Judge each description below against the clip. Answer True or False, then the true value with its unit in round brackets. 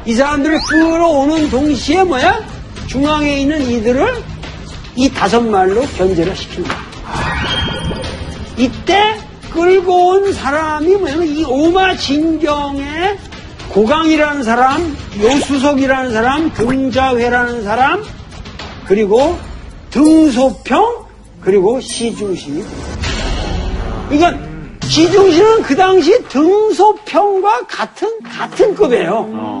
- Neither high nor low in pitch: False (300 Hz)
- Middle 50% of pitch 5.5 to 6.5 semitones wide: True (6.0 semitones)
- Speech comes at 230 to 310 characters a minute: False (220 characters per minute)